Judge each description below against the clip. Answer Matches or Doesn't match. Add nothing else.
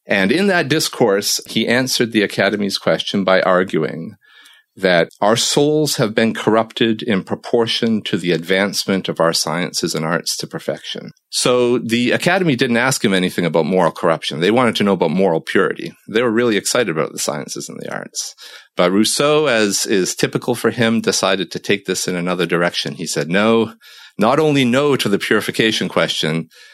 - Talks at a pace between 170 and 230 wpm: Matches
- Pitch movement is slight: Doesn't match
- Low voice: Matches